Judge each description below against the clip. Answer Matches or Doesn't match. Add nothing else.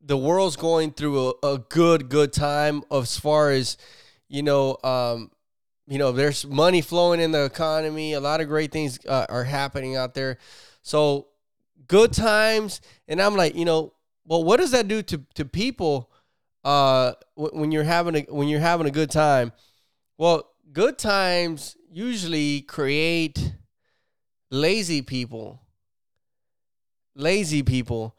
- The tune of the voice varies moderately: Matches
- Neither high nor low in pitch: Matches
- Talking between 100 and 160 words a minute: Matches